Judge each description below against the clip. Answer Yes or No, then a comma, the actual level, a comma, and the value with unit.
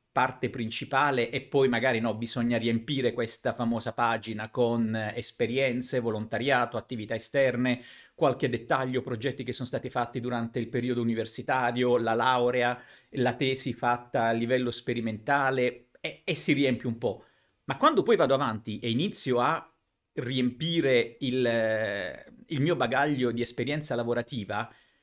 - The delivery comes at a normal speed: Yes, average, 135 wpm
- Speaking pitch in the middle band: No, low, 125 Hz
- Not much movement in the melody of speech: Yes, narrow, 2.2 semitones